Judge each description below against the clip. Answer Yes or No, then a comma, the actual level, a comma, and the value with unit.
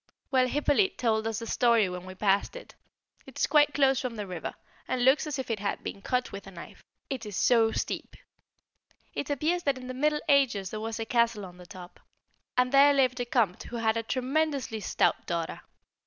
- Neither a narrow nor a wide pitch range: Yes, average, 4.6 semitones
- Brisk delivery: Yes, fast, 215 wpm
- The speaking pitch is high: Yes, high, 240 Hz